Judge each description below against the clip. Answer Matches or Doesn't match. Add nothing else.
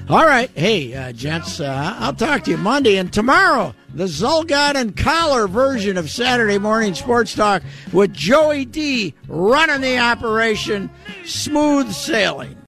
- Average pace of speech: Matches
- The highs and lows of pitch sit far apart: Matches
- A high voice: Matches